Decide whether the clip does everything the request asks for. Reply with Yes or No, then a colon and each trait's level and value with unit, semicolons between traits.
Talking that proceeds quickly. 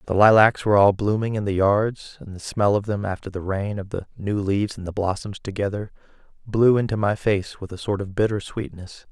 Yes: fast, 225 wpm